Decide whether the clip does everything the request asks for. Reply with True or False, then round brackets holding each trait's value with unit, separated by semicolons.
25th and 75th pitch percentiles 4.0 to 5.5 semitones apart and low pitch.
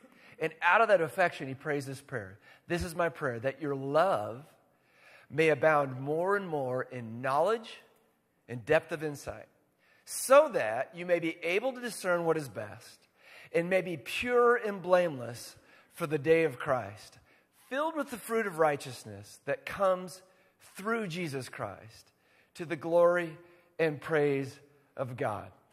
False (5.1 semitones; 160 Hz)